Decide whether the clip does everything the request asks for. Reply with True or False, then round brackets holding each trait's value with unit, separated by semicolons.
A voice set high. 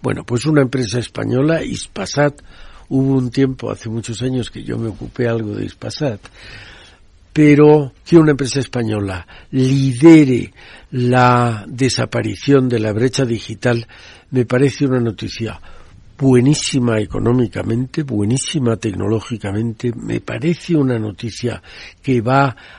False (120 Hz)